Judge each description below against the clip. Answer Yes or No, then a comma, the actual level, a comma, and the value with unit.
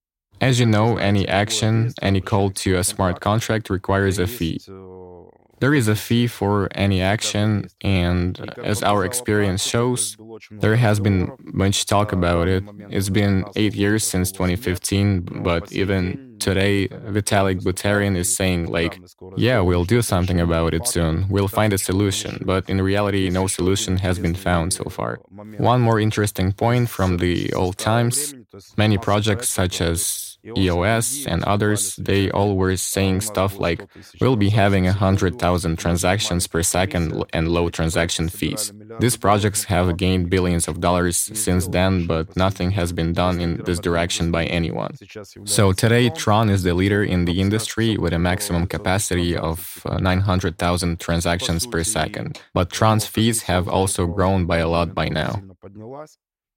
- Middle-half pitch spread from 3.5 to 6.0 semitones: No, average, 2.9 semitones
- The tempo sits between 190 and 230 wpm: No, average, 160 wpm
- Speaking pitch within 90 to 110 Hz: Yes, very low, 95 Hz